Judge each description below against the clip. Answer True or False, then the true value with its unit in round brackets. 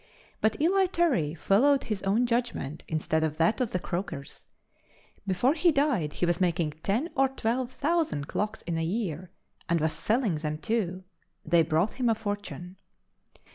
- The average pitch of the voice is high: True (200 Hz)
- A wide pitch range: True (7.2 semitones)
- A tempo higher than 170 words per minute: False (165 wpm)